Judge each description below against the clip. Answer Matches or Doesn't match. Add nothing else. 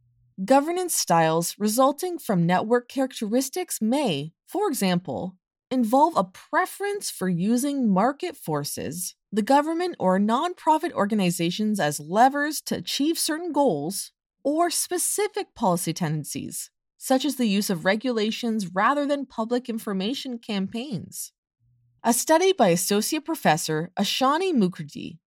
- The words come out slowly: Matches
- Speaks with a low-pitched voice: Doesn't match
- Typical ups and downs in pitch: Doesn't match